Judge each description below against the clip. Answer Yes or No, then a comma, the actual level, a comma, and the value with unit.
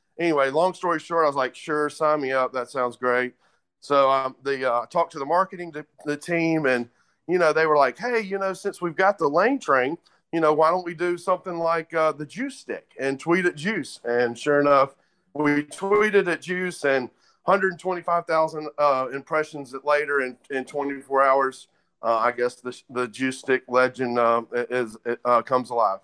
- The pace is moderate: Yes, average, 195 wpm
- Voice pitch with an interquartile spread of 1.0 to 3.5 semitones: No, average, 5.0 semitones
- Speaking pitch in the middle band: Yes, medium, 145 Hz